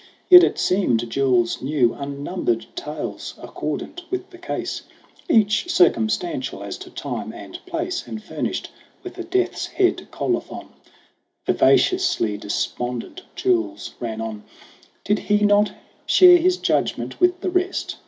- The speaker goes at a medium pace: No, slow, 130 wpm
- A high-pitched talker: Yes, high, 215 Hz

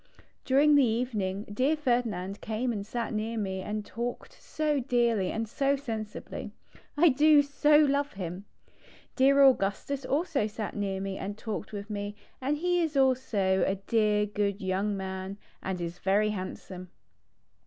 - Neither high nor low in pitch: No, high, 220 Hz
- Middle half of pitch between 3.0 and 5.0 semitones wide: No, wide, 5.4 semitones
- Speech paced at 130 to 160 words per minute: Yes, average, 155 wpm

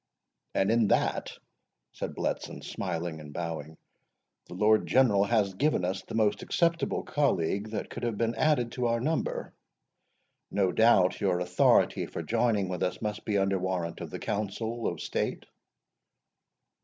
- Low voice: Yes, low, 105 Hz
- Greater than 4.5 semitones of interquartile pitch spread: No, average, 4.2 semitones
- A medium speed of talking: Yes, average, 155 wpm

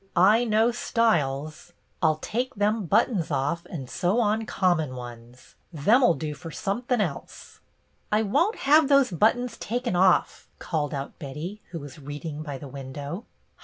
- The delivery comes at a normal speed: Yes, average, 165 wpm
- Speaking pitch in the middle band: Yes, medium, 175 Hz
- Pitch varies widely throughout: Yes, wide, 7.4 semitones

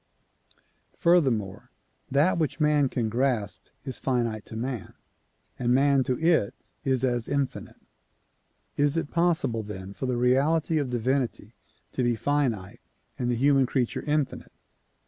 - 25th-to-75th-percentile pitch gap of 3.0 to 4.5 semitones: Yes, average, 3.4 semitones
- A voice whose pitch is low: Yes, low, 130 Hz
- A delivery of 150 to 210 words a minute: No, slow, 135 wpm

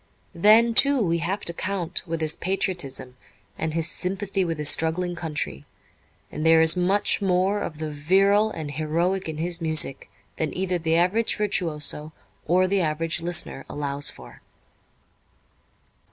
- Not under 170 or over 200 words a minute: No, average, 150 wpm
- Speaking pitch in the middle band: Yes, medium, 170 Hz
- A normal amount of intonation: Yes, average, 3.4 semitones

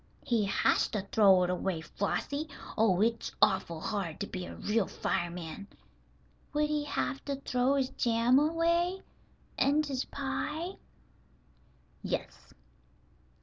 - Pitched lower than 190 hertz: No, high, 235 Hz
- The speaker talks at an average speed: No, slow, 125 wpm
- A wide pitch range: Yes, wide, 7.0 semitones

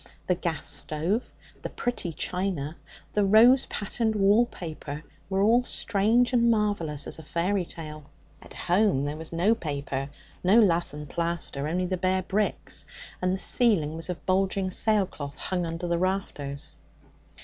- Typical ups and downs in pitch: Yes, average, 4.4 semitones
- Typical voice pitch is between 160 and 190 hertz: Yes, medium, 185 Hz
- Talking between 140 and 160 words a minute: Yes, average, 155 wpm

